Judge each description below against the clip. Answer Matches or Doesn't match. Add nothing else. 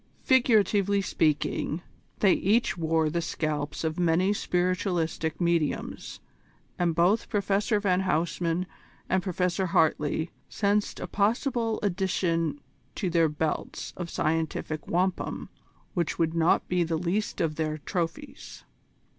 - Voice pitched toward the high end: Doesn't match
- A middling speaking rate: Doesn't match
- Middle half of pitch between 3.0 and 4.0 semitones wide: Matches